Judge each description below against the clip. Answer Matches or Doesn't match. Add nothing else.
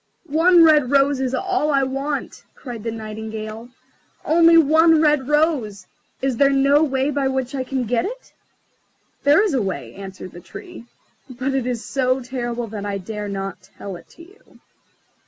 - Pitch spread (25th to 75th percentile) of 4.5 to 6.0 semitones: Matches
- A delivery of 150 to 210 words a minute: Matches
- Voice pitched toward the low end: Doesn't match